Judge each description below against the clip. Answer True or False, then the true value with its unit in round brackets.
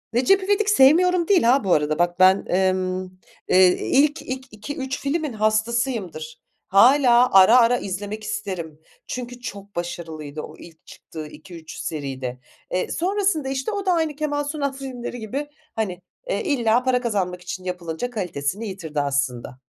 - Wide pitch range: True (7.5 semitones)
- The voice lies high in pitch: True (215 Hz)